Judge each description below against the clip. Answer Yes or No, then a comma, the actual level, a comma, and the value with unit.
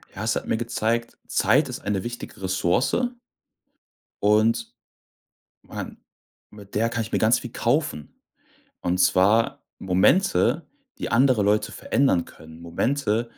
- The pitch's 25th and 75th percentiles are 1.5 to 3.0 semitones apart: No, average, 3.7 semitones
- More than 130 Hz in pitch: No, low, 110 Hz